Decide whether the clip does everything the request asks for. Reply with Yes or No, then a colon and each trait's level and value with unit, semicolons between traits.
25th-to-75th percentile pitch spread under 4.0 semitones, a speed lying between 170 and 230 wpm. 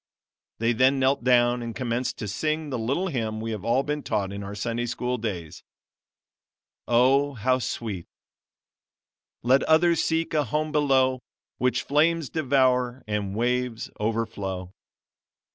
No: average, 3.6 semitones; average, 140 wpm